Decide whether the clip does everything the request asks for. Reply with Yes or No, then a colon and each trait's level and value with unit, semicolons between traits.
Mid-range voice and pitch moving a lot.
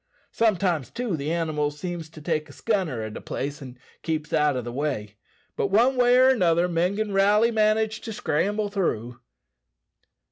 Yes: medium, 170 Hz; wide, 6.2 semitones